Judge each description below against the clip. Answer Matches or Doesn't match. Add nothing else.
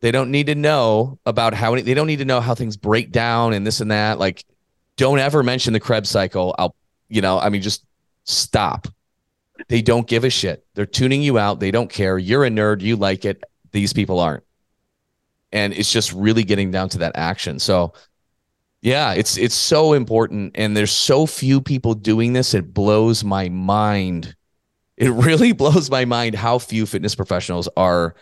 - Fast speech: Doesn't match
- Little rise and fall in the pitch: Doesn't match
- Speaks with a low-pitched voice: Matches